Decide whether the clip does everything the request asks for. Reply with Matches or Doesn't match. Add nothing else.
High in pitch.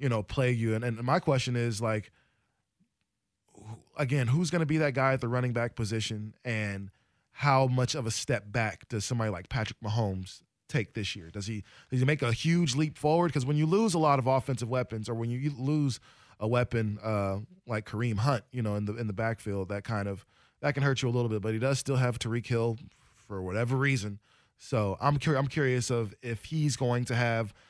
Doesn't match